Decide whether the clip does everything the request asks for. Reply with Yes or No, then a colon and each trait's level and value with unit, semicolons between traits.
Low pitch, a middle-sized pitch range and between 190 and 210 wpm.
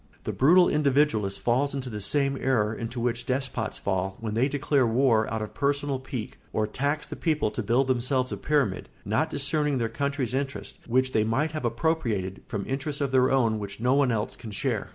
Yes: low, 130 Hz; average, 4.1 semitones; average, 200 wpm